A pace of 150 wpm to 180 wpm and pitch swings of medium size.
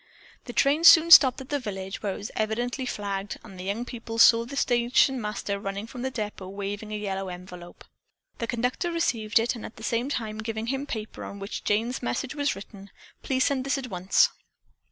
No: fast, 205 wpm; average, 4.1 semitones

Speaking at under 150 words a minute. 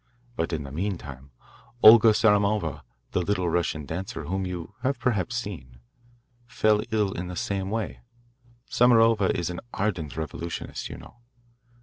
Yes: average, 140 wpm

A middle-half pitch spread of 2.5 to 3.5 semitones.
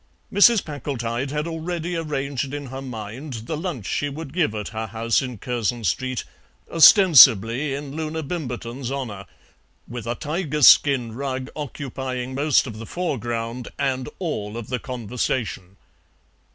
No: average, 4.2 semitones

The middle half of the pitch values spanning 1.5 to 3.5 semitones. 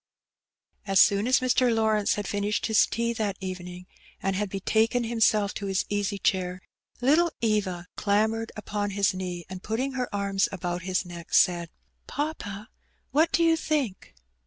Yes: average, 3.2 semitones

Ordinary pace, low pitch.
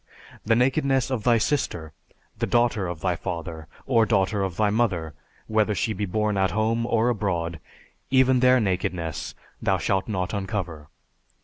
Yes: average, 155 wpm; low, 105 Hz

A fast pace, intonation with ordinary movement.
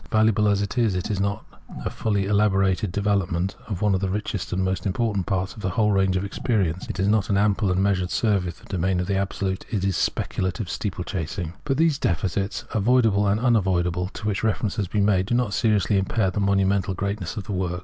No: fast, 220 wpm; narrow, 2.2 semitones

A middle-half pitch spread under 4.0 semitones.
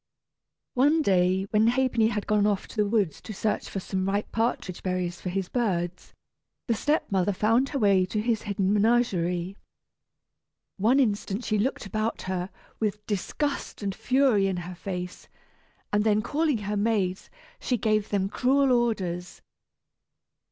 Yes: average, 3.5 semitones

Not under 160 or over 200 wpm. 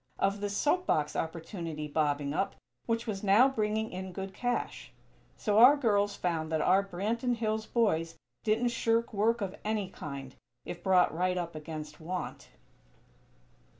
No: average, 150 wpm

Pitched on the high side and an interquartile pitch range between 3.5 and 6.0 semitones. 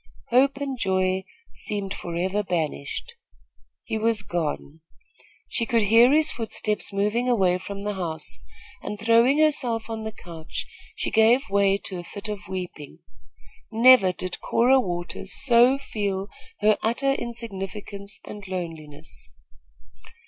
Yes: high, 205 Hz; average, 4.0 semitones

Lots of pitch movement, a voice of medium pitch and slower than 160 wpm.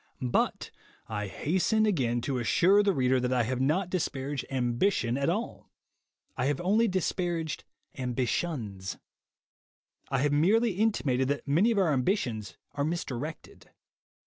Yes: wide, 6.6 semitones; medium, 145 Hz; average, 140 wpm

